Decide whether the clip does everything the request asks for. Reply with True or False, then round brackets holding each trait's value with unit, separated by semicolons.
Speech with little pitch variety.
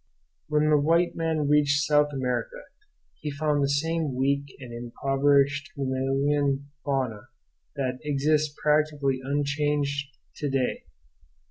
True (1.5 semitones)